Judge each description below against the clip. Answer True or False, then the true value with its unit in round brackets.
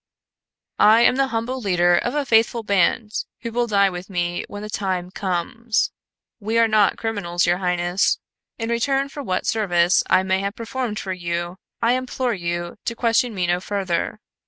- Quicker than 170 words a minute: True (180 wpm)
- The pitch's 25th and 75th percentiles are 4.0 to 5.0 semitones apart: True (4.6 semitones)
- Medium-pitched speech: False (205 Hz)